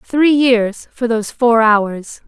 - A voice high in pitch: Yes, high, 235 Hz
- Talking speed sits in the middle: Yes, average, 160 wpm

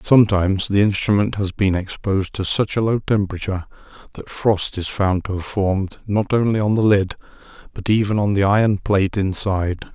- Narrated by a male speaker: Yes, male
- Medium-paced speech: Yes, average, 180 wpm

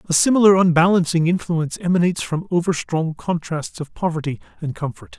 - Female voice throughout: No, male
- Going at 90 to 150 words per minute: Yes, average, 140 wpm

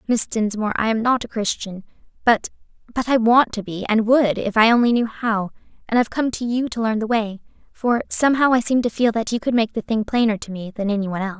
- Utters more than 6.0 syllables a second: Yes, 6.2 syllables/s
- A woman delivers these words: Yes, female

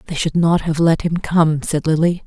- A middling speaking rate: No, fast, 240 wpm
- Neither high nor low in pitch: Yes, medium, 160 Hz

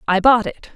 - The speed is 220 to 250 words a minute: Yes, fast, 240 wpm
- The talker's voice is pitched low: No, high, 220 Hz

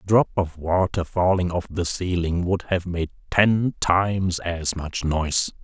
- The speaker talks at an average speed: Yes, average, 170 wpm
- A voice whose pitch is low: Yes, very low, 90 Hz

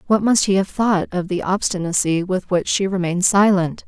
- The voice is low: No, high, 190 Hz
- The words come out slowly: No, average, 200 wpm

